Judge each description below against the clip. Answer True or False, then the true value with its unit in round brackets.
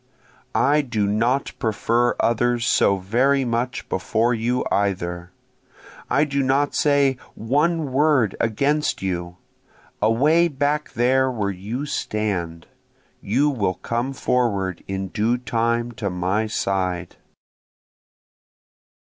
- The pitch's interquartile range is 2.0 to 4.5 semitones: False (5.2 semitones)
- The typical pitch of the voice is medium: False (115 Hz)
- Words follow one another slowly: True (110 wpm)